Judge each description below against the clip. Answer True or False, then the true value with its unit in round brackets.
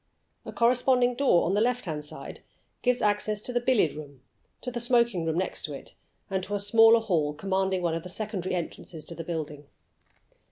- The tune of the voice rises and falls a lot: True (6.1 semitones)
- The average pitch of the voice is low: False (195 Hz)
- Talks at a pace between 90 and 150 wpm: False (195 wpm)